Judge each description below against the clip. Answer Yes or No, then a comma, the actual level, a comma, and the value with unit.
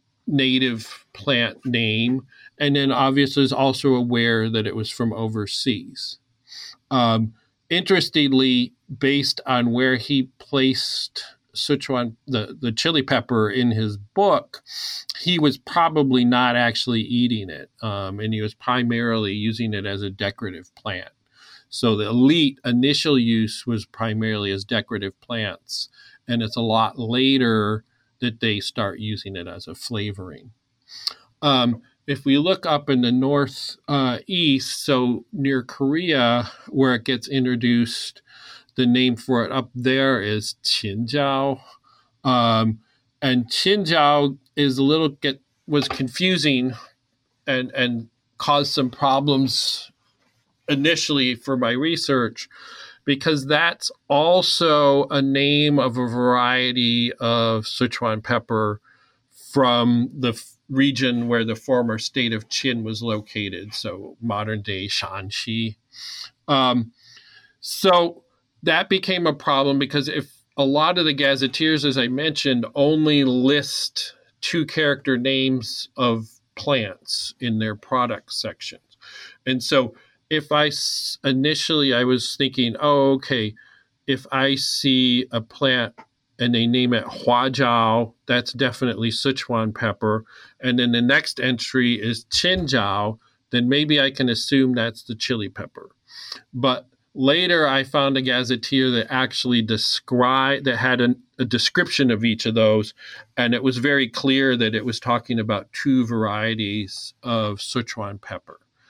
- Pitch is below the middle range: Yes, low, 125 Hz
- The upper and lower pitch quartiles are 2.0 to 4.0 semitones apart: Yes, average, 3.2 semitones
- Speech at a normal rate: No, slow, 130 wpm